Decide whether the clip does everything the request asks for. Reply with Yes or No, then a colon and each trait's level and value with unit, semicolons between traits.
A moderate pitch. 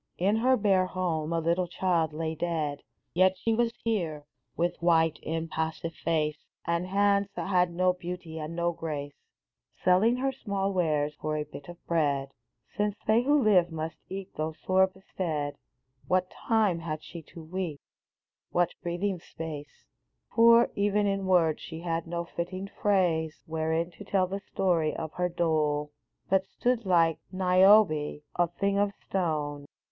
Yes: medium, 175 Hz